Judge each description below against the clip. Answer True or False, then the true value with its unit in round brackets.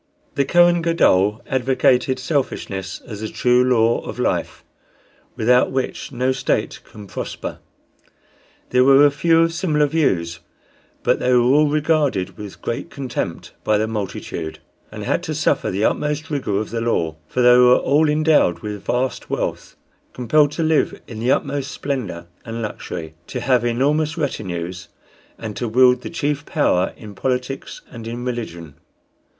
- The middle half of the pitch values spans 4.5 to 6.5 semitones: True (5.2 semitones)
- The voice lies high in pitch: False (125 Hz)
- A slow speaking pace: False (155 wpm)